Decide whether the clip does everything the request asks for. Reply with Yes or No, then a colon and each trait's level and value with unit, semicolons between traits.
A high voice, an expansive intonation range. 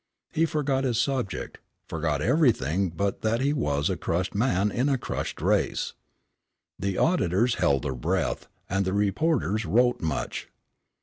No: low, 105 Hz; wide, 7.3 semitones